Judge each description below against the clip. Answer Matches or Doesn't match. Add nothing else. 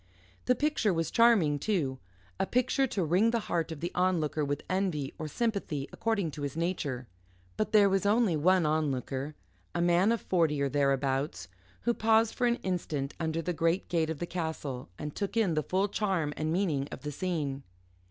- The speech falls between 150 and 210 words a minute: Matches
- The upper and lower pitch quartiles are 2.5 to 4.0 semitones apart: Doesn't match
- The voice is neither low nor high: Matches